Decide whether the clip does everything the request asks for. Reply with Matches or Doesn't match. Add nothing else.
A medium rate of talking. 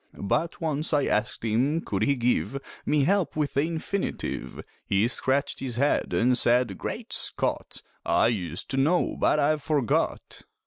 Matches